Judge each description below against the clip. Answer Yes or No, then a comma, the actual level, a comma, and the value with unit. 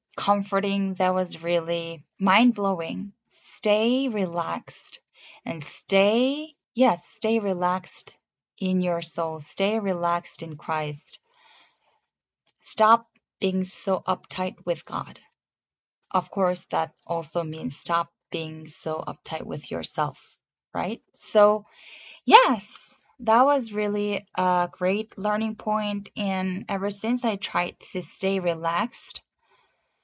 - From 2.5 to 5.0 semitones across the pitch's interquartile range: Yes, average, 3.6 semitones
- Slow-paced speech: Yes, slow, 110 wpm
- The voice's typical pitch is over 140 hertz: Yes, high, 190 Hz